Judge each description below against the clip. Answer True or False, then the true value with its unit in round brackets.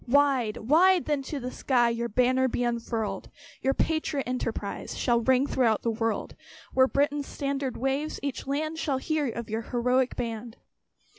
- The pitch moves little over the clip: False (3.1 semitones)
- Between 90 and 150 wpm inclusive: False (160 wpm)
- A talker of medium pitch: False (260 Hz)